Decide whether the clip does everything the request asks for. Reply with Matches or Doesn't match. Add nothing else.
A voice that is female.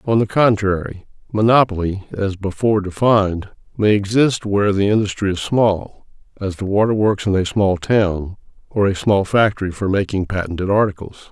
Doesn't match